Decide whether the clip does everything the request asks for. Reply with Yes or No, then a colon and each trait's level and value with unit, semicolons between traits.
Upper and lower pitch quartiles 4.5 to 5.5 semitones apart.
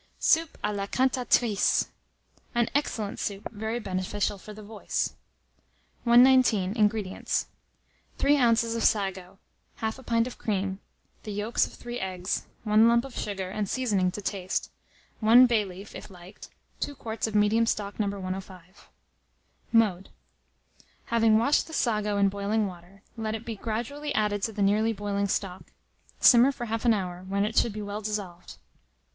No: average, 2.7 semitones